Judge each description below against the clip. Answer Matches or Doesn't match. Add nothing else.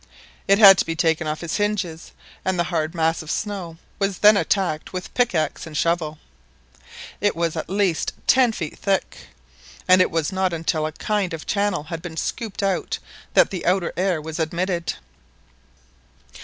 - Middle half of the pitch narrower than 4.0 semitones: Matches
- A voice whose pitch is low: Doesn't match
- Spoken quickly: Doesn't match